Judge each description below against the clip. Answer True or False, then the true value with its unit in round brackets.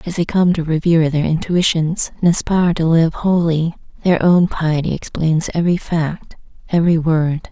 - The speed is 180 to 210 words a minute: False (160 wpm)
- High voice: False (165 Hz)